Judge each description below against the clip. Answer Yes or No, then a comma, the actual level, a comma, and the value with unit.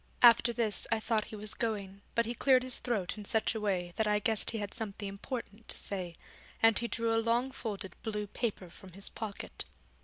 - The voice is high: Yes, high, 220 Hz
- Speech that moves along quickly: Yes, fast, 215 wpm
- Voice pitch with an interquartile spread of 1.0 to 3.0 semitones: Yes, narrow, 2.6 semitones